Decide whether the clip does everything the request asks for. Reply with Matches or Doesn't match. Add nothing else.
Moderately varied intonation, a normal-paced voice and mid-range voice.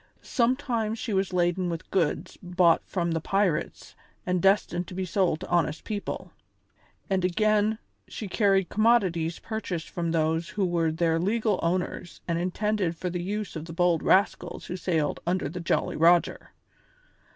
Matches